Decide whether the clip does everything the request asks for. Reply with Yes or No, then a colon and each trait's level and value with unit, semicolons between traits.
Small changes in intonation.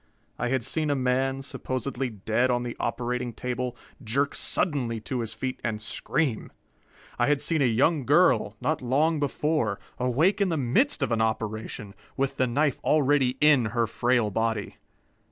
No: average, 3.6 semitones